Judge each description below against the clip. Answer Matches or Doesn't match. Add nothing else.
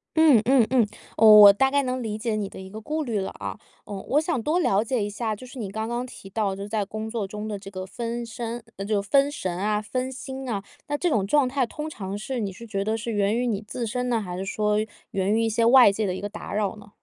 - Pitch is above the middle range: Matches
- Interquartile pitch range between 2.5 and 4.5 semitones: Matches